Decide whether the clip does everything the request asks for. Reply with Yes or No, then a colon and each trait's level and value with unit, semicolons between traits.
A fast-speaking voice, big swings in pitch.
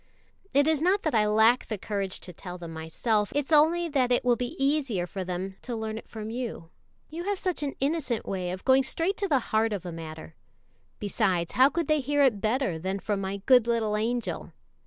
Yes: fast, 220 wpm; wide, 6.3 semitones